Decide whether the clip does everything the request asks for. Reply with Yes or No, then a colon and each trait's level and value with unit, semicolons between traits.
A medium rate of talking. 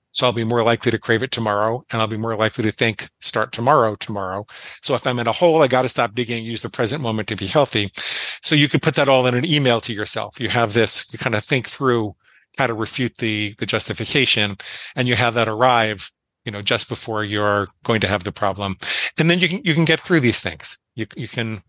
No: fast, 255 wpm